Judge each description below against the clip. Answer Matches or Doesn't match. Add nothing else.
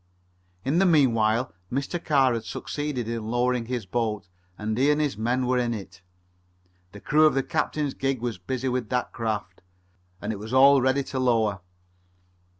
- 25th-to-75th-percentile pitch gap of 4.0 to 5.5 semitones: Doesn't match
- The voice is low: Matches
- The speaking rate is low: Doesn't match